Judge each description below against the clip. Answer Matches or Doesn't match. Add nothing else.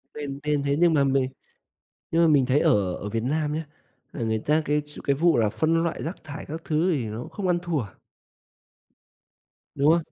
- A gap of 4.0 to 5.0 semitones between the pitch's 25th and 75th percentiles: Doesn't match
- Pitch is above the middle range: Doesn't match